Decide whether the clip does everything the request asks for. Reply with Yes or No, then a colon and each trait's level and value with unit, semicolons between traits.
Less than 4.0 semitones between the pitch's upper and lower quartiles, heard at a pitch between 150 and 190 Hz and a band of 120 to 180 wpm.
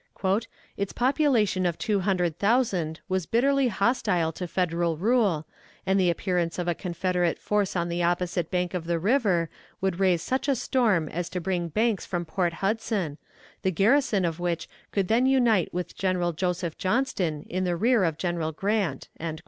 Yes: average, 3.6 semitones; medium, 185 Hz; average, 170 wpm